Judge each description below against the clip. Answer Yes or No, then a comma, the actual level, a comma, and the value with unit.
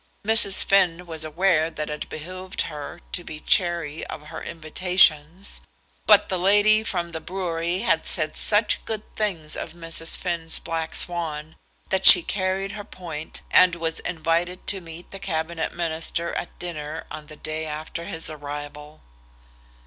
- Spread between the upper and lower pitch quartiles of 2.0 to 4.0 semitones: Yes, average, 2.8 semitones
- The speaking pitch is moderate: Yes, medium, 170 Hz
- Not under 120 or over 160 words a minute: Yes, average, 155 wpm